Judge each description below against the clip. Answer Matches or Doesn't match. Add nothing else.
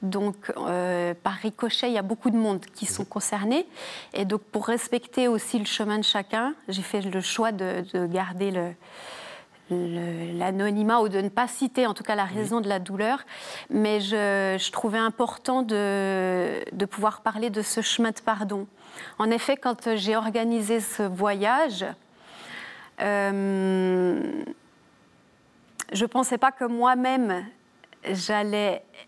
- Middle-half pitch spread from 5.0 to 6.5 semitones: Doesn't match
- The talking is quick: Doesn't match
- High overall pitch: Matches